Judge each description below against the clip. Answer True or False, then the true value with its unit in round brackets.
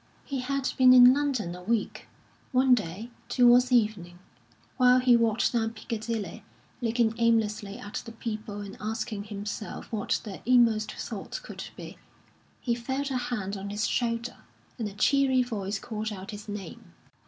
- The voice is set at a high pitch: True (225 Hz)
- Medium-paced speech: True (155 wpm)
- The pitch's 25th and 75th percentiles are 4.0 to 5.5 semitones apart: False (3.2 semitones)